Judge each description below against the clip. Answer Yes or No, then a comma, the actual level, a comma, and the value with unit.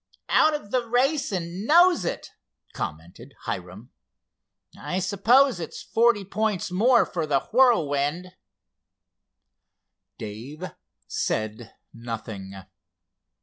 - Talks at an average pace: No, slow, 95 wpm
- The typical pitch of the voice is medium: Yes, medium, 180 Hz